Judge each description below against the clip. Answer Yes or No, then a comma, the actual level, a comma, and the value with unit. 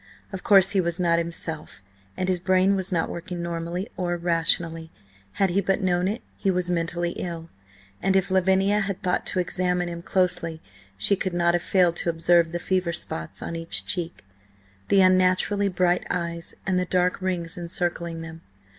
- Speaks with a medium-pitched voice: Yes, medium, 175 Hz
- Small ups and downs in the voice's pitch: Yes, narrow, 1.8 semitones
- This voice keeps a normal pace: Yes, average, 180 wpm